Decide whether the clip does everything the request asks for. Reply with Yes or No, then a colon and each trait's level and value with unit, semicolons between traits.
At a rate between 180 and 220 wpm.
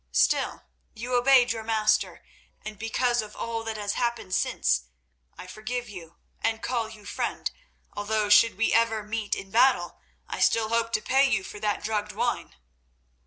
No: average, 165 wpm